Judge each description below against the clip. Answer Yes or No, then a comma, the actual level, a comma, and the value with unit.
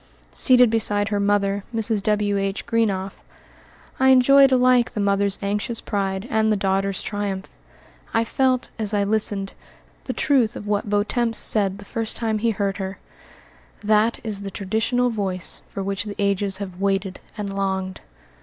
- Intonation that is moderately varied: No, narrow, 2.3 semitones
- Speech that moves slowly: No, average, 155 wpm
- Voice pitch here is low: No, high, 205 Hz